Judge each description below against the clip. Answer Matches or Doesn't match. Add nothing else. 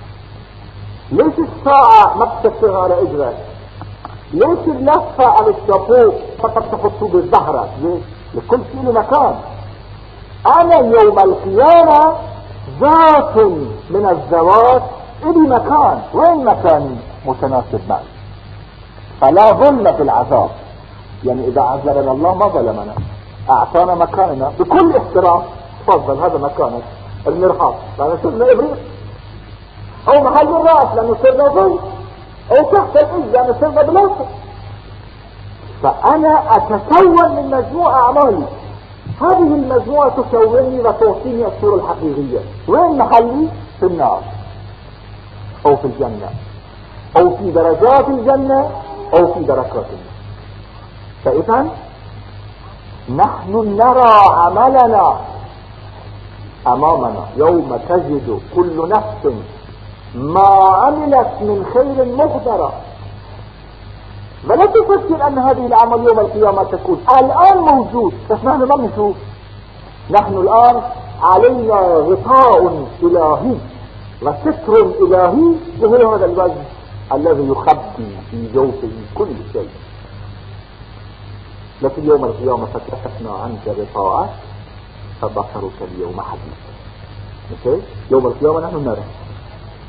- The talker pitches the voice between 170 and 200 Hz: Doesn't match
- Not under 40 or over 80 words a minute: Doesn't match